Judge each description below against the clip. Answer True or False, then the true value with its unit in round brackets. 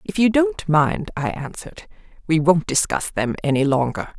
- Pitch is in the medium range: True (165 Hz)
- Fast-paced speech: False (170 wpm)